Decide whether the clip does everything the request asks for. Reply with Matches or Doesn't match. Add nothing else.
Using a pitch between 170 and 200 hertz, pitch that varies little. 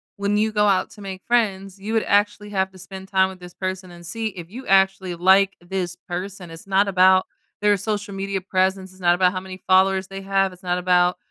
Matches